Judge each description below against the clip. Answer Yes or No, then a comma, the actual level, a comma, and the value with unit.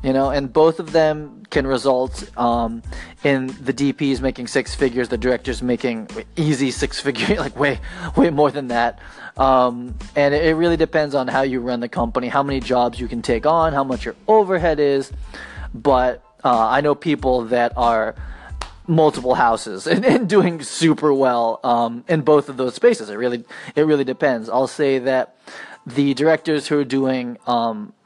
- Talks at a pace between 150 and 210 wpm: Yes, average, 180 wpm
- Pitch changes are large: No, average, 3.6 semitones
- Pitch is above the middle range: No, low, 135 Hz